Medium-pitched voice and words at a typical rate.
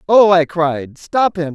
Yes: medium, 170 Hz; average, 195 wpm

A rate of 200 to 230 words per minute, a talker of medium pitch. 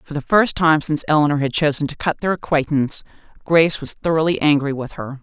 Yes: fast, 205 wpm; medium, 150 Hz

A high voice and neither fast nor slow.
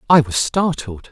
No: medium, 140 Hz; average, 160 wpm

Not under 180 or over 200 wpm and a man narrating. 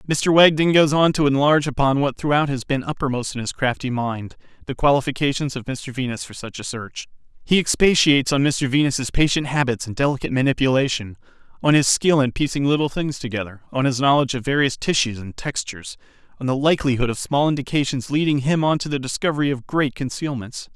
Yes: average, 190 wpm; male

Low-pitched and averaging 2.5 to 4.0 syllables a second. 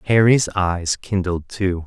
Yes: very low, 95 Hz; 3.7 syllables/s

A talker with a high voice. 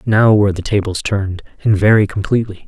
No: low, 100 Hz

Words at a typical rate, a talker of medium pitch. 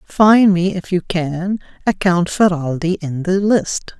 Yes: average, 165 wpm; medium, 180 Hz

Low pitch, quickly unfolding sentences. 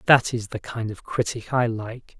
Yes: low, 115 Hz; fast, 220 wpm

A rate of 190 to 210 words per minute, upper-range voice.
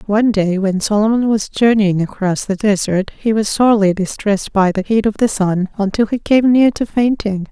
Yes: average, 200 wpm; high, 210 Hz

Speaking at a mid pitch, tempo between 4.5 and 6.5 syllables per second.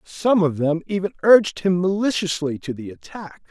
Yes: medium, 170 Hz; 5.0 syllables/s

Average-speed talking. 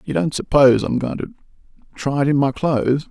Yes: average, 195 wpm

